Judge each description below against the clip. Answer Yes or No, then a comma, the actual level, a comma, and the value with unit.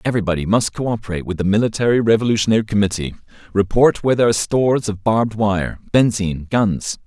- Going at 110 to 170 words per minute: Yes, average, 155 wpm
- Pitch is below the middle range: Yes, low, 105 Hz